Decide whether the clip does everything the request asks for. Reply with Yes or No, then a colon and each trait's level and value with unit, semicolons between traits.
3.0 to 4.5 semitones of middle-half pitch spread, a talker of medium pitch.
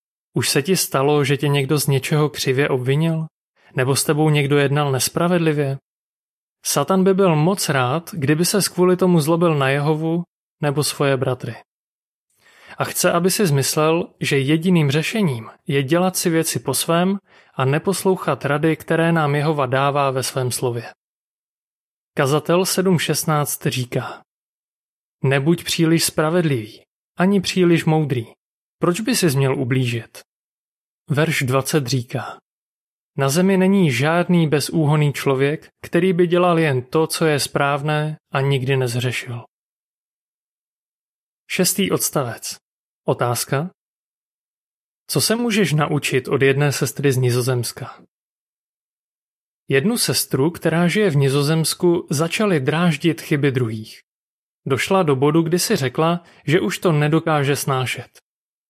Yes: average, 3.9 semitones; medium, 150 Hz